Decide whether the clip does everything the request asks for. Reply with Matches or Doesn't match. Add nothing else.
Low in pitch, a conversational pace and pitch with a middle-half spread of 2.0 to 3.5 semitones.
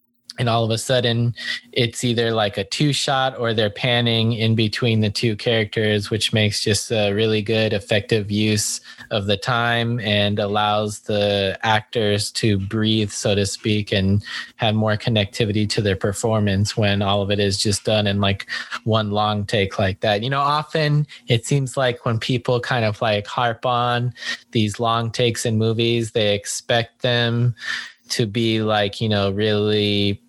Matches